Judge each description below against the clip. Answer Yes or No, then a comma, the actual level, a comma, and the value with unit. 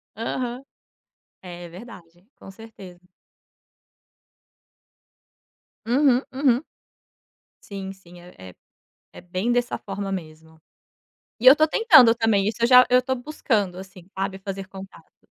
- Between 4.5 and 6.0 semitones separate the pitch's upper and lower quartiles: Yes, average, 5.0 semitones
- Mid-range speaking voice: No, high, 200 Hz